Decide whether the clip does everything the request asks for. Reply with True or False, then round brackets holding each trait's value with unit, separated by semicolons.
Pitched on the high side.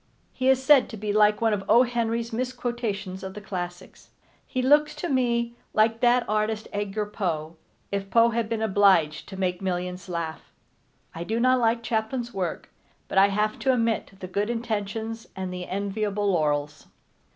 True (215 Hz)